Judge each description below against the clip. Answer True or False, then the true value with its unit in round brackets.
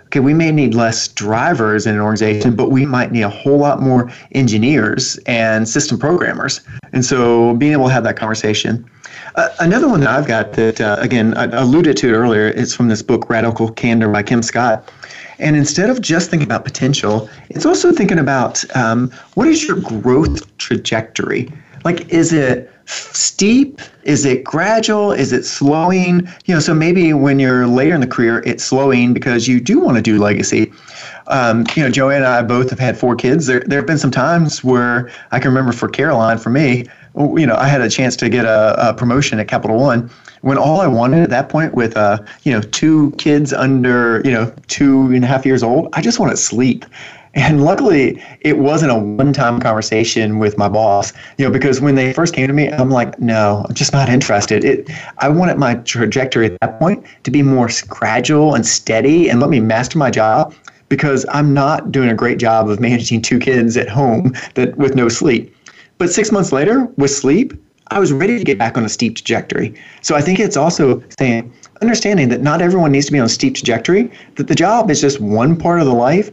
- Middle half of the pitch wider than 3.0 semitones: True (4.1 semitones)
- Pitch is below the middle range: True (130 Hz)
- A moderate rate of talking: False (215 wpm)